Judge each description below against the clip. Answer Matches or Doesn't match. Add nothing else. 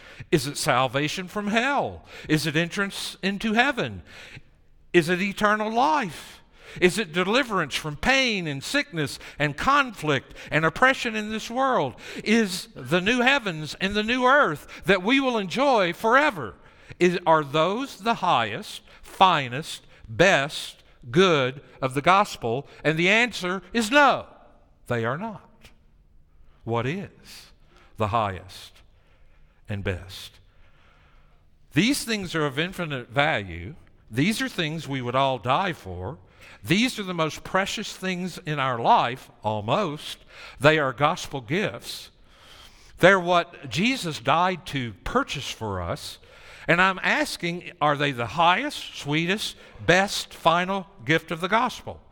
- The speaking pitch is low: Doesn't match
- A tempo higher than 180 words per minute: Doesn't match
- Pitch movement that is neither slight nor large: Doesn't match